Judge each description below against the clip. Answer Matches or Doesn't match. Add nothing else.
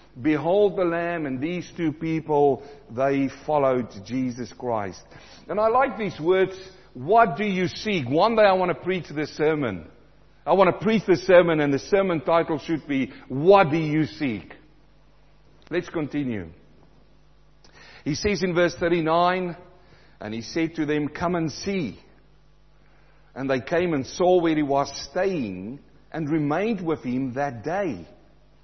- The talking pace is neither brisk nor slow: Matches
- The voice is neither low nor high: Matches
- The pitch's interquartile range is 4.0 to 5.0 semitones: Matches